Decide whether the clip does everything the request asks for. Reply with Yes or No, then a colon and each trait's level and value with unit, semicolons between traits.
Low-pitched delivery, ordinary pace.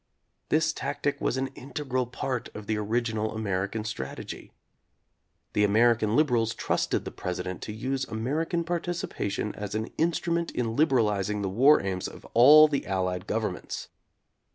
Yes: low, 115 Hz; average, 150 wpm